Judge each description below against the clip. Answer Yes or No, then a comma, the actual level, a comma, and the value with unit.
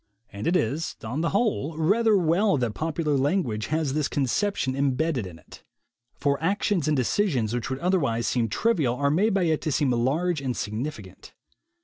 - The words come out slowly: No, average, 180 wpm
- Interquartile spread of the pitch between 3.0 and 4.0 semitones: No, wide, 5.6 semitones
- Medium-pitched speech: Yes, medium, 150 Hz